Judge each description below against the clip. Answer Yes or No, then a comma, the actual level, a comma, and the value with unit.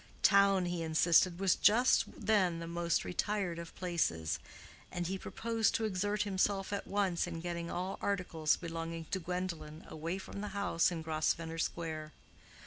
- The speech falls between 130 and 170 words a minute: Yes, average, 155 wpm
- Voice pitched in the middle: Yes, medium, 175 Hz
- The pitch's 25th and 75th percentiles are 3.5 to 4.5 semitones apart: No, average, 3.0 semitones